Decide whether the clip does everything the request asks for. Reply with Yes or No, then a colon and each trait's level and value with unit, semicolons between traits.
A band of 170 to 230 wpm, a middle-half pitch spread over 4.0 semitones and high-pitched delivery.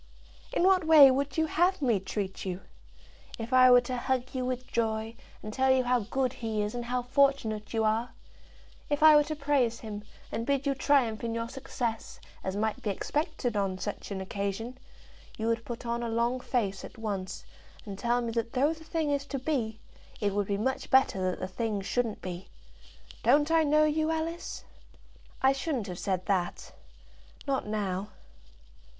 Yes: average, 190 wpm; average, 4.5 semitones; high, 240 Hz